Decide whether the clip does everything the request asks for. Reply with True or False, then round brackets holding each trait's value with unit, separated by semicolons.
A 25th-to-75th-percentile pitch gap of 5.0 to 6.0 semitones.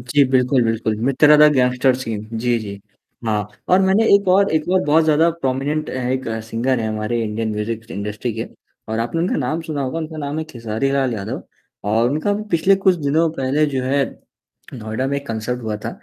True (5.3 semitones)